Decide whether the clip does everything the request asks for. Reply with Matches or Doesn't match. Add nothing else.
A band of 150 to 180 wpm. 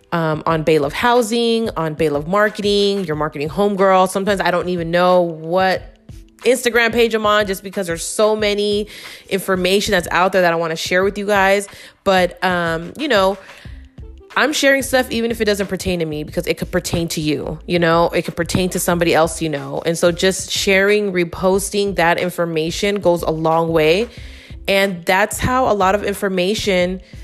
Doesn't match